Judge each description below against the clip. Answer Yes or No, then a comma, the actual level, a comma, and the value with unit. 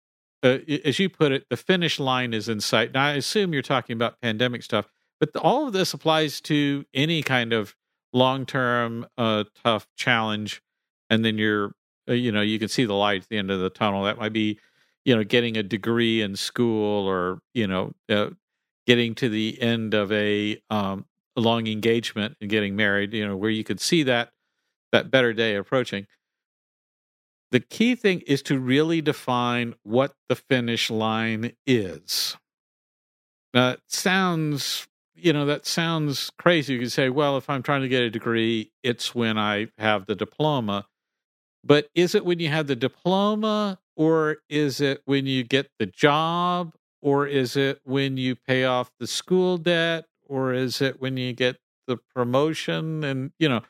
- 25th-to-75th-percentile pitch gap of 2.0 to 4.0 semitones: No, average, 4.7 semitones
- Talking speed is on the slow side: No, average, 180 wpm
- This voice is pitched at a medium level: No, low, 125 Hz